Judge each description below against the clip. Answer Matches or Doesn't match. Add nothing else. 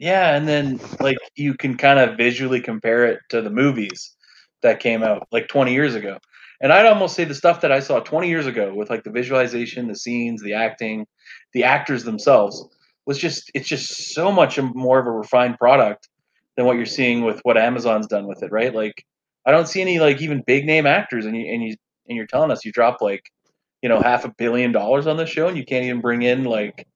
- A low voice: Matches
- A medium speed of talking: Doesn't match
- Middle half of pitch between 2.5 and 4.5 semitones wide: Matches